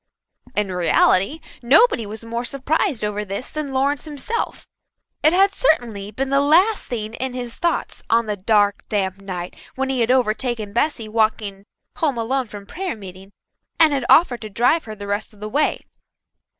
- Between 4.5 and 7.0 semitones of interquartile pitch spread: Yes, average, 5.1 semitones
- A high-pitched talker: Yes, high, 235 Hz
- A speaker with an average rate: Yes, average, 175 wpm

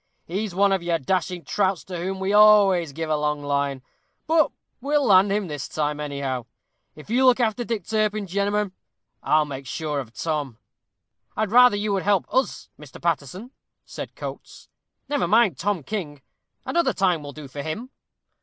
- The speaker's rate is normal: Yes, average, 175 wpm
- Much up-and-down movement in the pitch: Yes, wide, 5.9 semitones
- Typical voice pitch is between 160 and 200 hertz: Yes, medium, 185 Hz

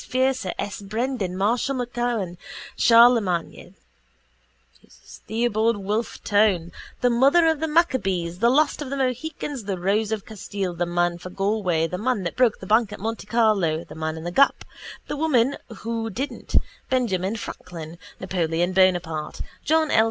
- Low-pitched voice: No, high, 215 Hz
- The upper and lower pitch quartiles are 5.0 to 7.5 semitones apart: Yes, wide, 5.4 semitones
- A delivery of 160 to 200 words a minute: No, average, 150 wpm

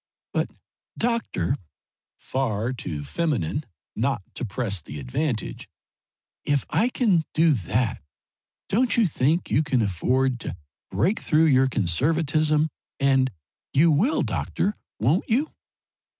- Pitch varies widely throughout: Yes, wide, 6.5 semitones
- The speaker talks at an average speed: No, slow, 120 wpm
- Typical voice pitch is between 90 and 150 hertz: Yes, low, 135 Hz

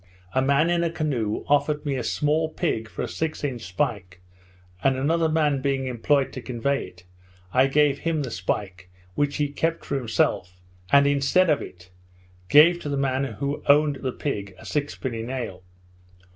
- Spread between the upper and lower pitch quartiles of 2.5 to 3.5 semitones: No, average, 3.9 semitones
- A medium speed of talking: Yes, average, 175 wpm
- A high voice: No, medium, 140 Hz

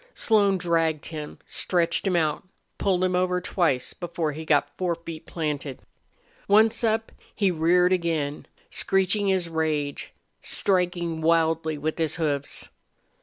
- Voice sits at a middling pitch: Yes, medium, 170 Hz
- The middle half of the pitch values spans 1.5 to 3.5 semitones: Yes, average, 2.7 semitones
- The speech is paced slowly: Yes, slow, 125 wpm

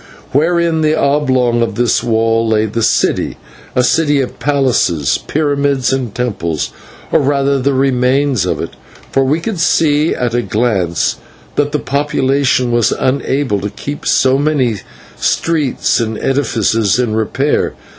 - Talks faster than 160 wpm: No, average, 145 wpm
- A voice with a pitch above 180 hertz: No, low, 130 Hz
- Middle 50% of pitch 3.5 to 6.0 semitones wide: Yes, average, 4.0 semitones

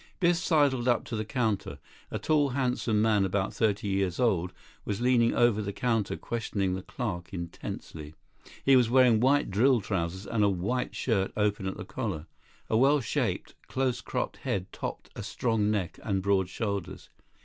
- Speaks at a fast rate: No, average, 170 wpm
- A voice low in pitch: Yes, low, 110 Hz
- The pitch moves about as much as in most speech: Yes, average, 4.3 semitones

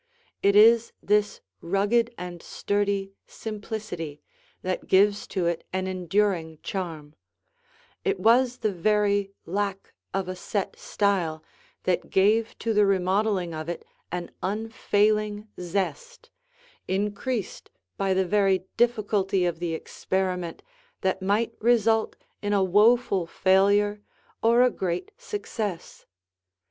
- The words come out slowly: Yes, slow, 115 wpm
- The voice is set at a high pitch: Yes, high, 200 Hz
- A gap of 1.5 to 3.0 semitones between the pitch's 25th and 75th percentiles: Yes, narrow, 2.6 semitones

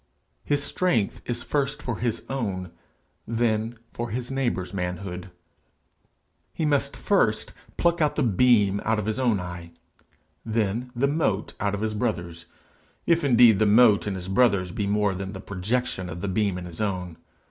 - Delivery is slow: No, average, 170 wpm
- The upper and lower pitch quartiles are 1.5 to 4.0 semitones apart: No, average, 4.6 semitones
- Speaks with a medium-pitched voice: No, low, 105 Hz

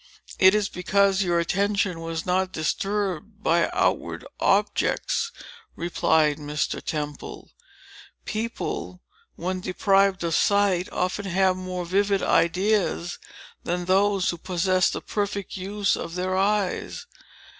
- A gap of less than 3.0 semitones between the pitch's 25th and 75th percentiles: Yes, narrow, 2.5 semitones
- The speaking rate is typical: No, slow, 115 wpm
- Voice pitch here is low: No, medium, 185 Hz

